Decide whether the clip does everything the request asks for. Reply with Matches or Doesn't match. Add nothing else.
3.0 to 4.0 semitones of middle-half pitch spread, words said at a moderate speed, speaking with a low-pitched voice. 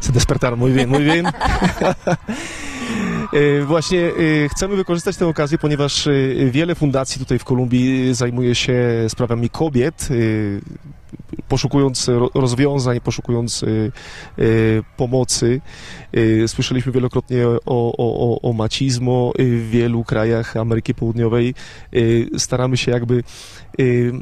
Doesn't match